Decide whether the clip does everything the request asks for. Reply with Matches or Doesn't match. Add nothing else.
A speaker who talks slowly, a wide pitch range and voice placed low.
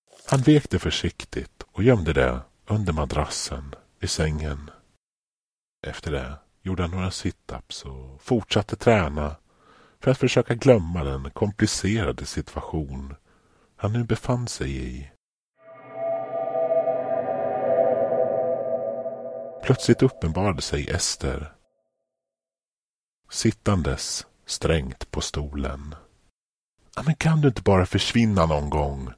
Matches